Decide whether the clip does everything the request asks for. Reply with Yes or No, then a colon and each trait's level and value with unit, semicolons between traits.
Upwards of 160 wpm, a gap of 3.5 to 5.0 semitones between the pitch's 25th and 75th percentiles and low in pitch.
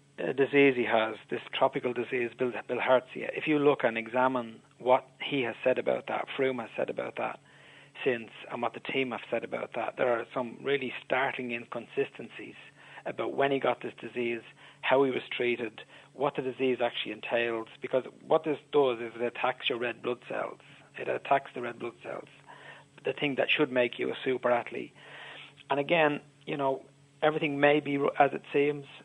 No: average, 190 wpm; average, 2.8 semitones; low, 130 Hz